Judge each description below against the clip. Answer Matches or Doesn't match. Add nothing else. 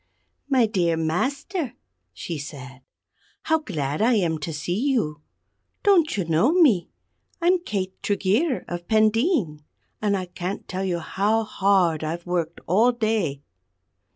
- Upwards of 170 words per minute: Doesn't match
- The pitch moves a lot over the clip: Matches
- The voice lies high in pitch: Matches